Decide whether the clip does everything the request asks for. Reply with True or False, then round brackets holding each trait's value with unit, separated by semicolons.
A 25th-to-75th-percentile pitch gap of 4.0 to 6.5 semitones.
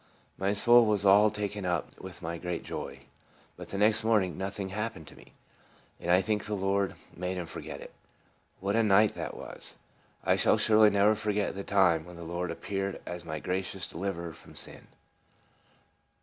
False (2.8 semitones)